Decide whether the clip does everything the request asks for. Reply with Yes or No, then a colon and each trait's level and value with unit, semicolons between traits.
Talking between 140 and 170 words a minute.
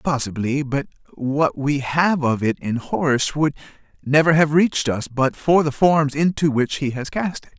No: average, 190 wpm